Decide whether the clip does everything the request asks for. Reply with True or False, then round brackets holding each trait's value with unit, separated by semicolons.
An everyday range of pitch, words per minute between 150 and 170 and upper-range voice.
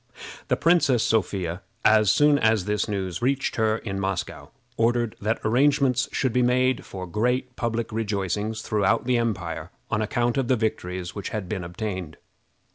False (4.1 semitones; 160 wpm; 110 Hz)